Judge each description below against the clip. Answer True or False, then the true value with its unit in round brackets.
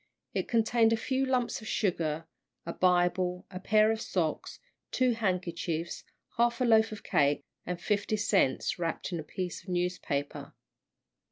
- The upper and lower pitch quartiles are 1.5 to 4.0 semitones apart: False (4.6 semitones)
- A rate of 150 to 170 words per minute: True (155 wpm)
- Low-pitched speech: False (185 Hz)